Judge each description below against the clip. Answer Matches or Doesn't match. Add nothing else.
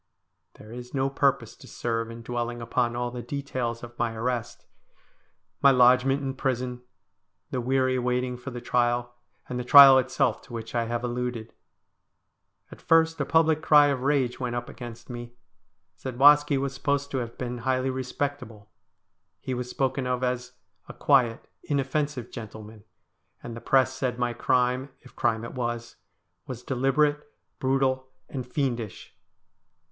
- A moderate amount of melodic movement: Doesn't match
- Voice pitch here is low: Matches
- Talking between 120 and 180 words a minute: Matches